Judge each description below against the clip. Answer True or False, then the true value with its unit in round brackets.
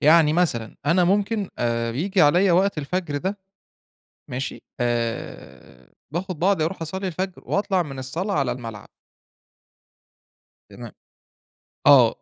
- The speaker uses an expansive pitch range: True (6.1 semitones)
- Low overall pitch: False (165 Hz)